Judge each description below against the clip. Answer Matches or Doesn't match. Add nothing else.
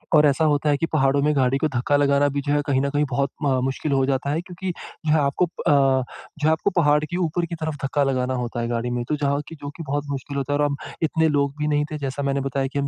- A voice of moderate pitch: Matches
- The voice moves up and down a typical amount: Doesn't match